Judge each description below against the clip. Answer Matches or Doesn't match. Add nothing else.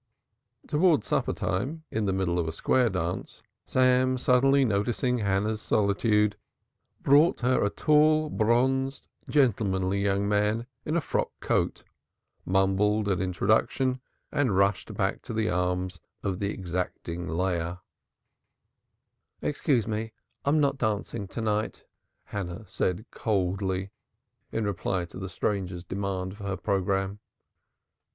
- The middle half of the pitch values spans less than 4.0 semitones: Doesn't match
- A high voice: Doesn't match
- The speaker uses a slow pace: Matches